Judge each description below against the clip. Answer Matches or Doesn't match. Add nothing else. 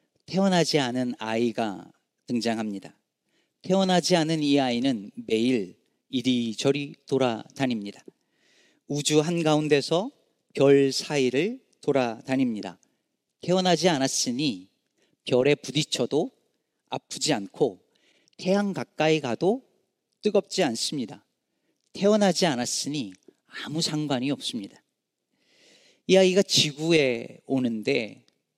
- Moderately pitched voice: Matches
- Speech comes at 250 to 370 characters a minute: Doesn't match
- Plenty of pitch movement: Matches